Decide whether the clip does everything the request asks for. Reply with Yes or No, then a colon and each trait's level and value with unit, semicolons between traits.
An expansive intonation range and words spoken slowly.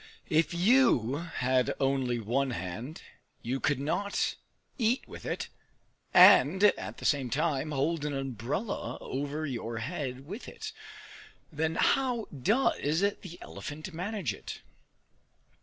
Yes: wide, 5.8 semitones; slow, 125 wpm